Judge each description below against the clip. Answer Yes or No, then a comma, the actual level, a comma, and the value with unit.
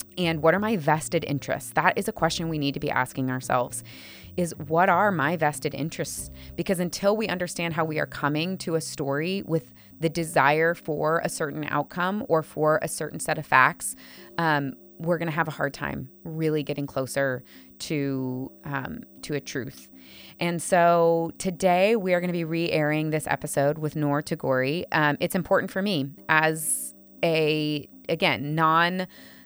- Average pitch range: Yes, average, 3.5 semitones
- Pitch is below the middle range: No, medium, 155 Hz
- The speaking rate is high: No, average, 170 wpm